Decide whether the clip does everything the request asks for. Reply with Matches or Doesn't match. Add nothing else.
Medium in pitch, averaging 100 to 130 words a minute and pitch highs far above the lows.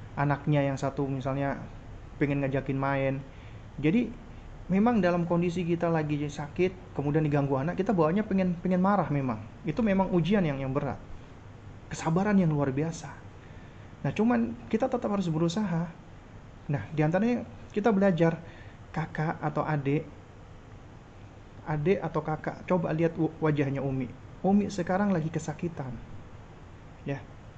Matches